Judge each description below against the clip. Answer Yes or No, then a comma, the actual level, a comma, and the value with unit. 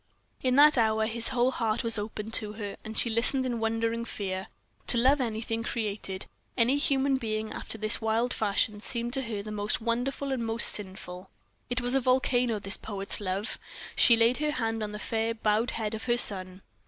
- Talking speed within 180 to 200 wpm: Yes, average, 190 wpm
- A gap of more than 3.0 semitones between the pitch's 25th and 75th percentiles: No, narrow, 2.4 semitones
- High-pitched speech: Yes, high, 225 Hz